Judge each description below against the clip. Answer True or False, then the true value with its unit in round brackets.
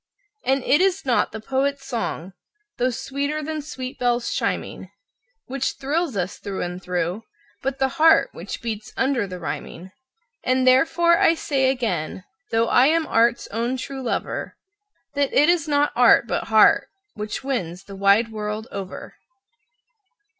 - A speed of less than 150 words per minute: False (155 wpm)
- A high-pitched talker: True (255 Hz)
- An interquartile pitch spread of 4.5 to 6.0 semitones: True (4.8 semitones)